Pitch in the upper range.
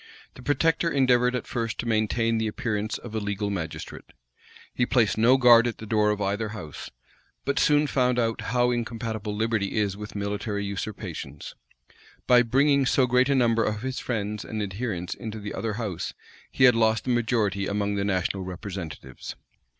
No: low, 110 Hz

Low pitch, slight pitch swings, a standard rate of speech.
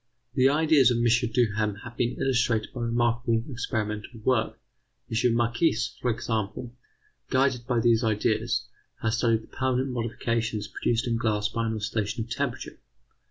Yes: low, 115 Hz; narrow, 1.8 semitones; average, 150 wpm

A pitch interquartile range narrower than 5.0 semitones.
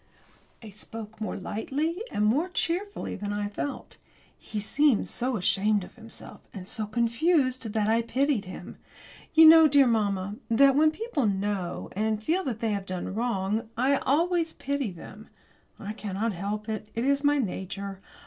No: wide, 5.4 semitones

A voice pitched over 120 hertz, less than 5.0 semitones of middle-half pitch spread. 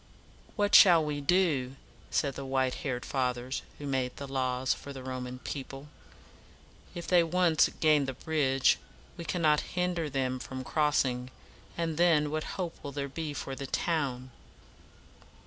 Yes: medium, 140 Hz; average, 3.4 semitones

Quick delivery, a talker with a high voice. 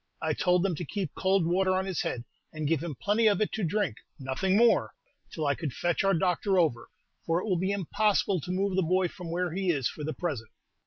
No: fast, 235 wpm; medium, 180 Hz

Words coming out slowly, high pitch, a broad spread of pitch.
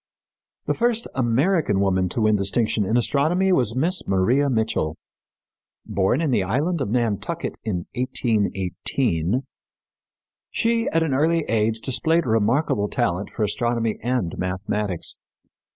No: slow, 125 wpm; low, 115 Hz; wide, 5.9 semitones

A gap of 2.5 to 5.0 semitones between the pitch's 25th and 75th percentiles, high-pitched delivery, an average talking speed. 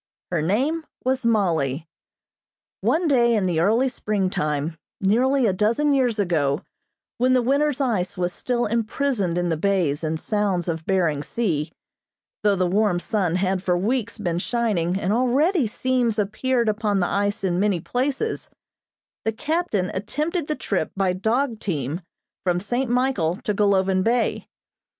No: wide, 5.6 semitones; high, 205 Hz; average, 150 wpm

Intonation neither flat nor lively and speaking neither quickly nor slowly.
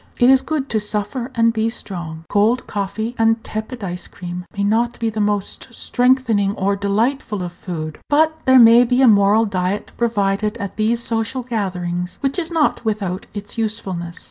Yes: average, 3.3 semitones; average, 175 wpm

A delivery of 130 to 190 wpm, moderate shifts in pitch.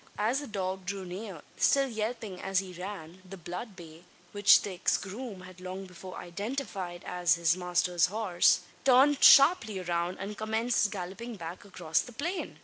Yes: average, 165 wpm; average, 3.6 semitones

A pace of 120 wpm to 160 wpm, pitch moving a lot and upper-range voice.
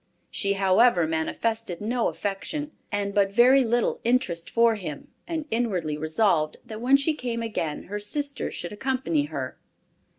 Yes: average, 145 wpm; wide, 5.9 semitones; high, 210 Hz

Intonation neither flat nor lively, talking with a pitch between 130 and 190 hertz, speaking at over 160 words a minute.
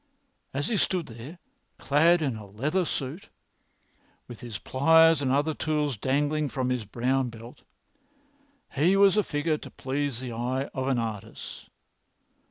No: average, 4.0 semitones; low, 135 Hz; average, 150 wpm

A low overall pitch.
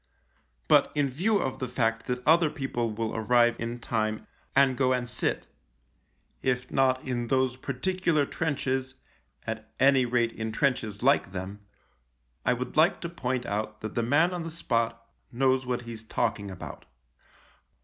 Yes: low, 125 Hz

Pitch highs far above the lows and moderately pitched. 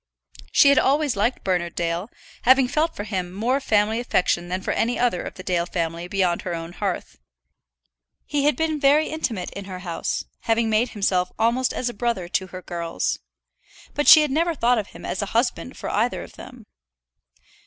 No: wide, 6.2 semitones; high, 210 Hz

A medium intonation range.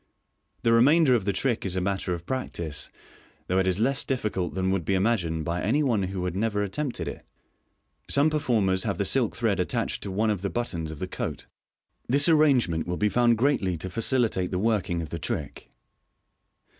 Yes: average, 4.8 semitones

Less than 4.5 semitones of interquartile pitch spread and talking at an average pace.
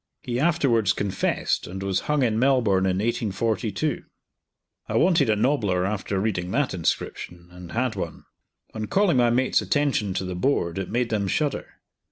No: wide, 5.5 semitones; average, 165 wpm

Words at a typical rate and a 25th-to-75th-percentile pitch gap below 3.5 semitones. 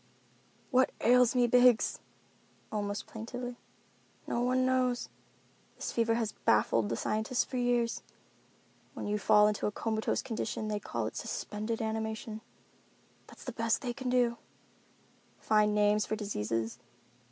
No: slow, 130 wpm; average, 2.7 semitones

